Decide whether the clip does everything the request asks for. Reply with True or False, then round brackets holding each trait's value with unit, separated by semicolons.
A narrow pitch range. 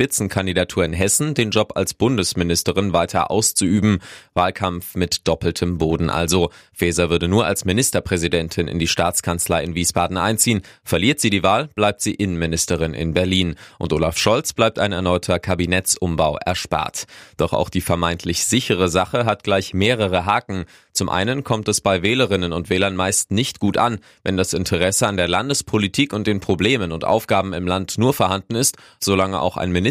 False (3.0 semitones)